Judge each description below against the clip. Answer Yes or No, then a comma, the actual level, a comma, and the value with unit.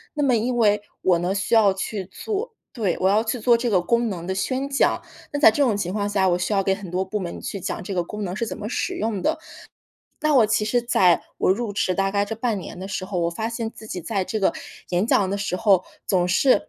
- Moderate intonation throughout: Yes, average, 3.6 semitones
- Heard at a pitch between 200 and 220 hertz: Yes, high, 205 Hz